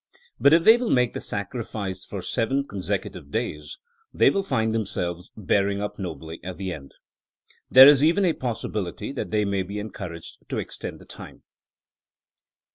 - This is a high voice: No, low, 105 Hz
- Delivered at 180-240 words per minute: No, average, 165 wpm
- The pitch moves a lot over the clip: Yes, wide, 5.9 semitones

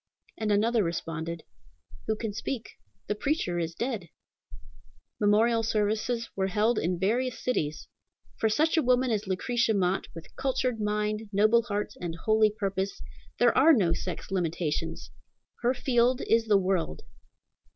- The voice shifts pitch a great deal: No, average, 3.8 semitones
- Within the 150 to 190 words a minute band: No, average, 140 wpm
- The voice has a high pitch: Yes, high, 215 Hz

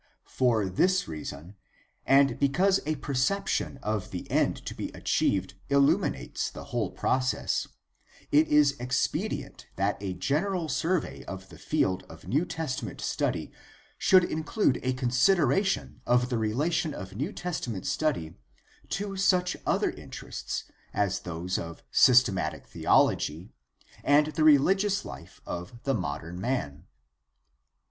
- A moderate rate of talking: No, slow, 125 wpm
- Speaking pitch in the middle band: No, low, 130 Hz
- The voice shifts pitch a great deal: Yes, wide, 8.6 semitones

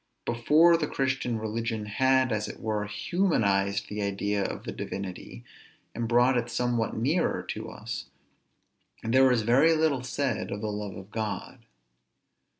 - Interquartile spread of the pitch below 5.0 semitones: Yes, average, 3.9 semitones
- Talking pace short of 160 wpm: Yes, average, 150 wpm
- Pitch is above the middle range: No, low, 115 Hz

